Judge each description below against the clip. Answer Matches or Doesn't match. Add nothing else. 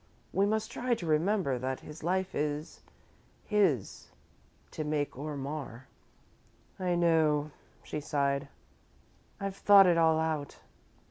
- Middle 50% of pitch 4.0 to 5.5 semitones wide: Matches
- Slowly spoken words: Matches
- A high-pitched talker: Doesn't match